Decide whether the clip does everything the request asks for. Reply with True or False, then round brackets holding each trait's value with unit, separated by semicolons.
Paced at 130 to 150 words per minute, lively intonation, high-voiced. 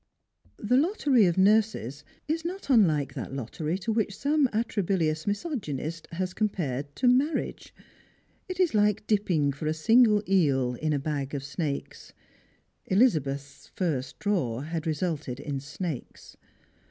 False (135 wpm; 7.2 semitones; 170 Hz)